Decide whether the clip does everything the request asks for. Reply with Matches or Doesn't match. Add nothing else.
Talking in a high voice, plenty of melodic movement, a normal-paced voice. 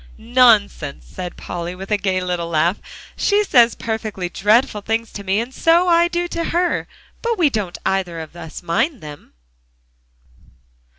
Matches